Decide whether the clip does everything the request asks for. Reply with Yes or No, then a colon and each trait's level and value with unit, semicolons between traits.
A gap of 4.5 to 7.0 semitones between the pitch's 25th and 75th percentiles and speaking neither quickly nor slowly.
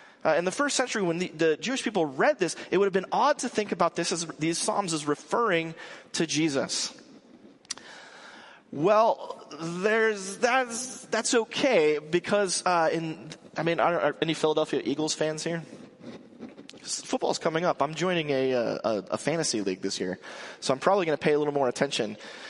Yes: wide, 5.6 semitones; average, 180 wpm